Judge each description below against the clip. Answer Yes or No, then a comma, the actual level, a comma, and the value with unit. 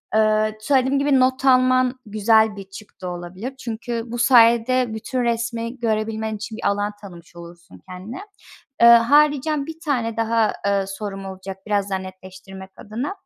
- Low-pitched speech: No, high, 220 Hz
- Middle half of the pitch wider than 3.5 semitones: Yes, average, 4.3 semitones